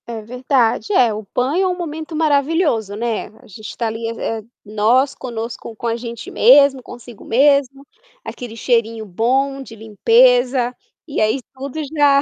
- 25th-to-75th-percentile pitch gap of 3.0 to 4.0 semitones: Yes, average, 3.6 semitones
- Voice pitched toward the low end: No, high, 245 Hz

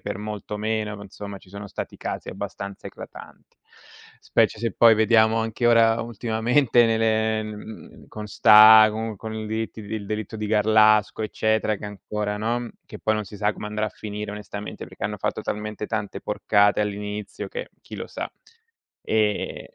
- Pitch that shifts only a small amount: Yes, narrow, 1.1 semitones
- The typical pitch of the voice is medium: No, low, 110 Hz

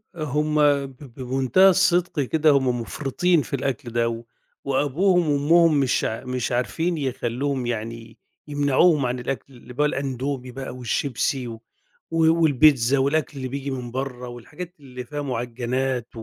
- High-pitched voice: No, low, 135 Hz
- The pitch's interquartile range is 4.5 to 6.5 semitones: No, average, 3.2 semitones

